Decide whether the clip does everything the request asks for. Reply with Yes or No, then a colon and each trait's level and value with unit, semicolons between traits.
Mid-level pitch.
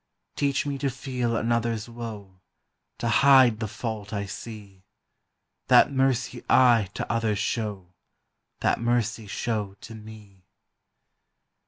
No: low, 115 Hz